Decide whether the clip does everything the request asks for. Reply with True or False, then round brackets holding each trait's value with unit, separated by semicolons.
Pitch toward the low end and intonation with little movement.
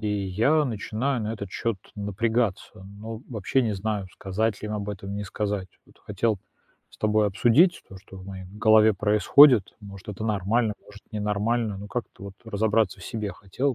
True (105 Hz; 2.1 semitones)